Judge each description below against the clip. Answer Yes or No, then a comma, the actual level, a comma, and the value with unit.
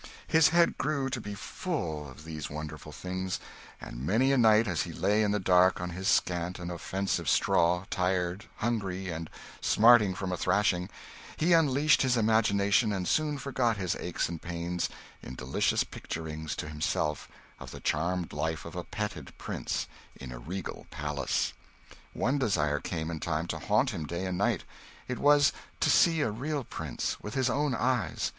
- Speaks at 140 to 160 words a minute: No, average, 175 wpm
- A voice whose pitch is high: No, very low, 95 Hz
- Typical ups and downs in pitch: No, wide, 6.5 semitones